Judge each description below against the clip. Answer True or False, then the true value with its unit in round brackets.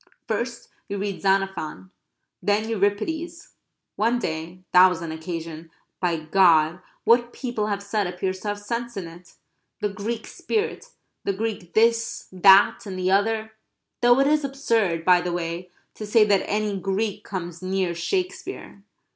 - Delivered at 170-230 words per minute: False (155 wpm)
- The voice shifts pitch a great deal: False (4.1 semitones)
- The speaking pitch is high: True (200 Hz)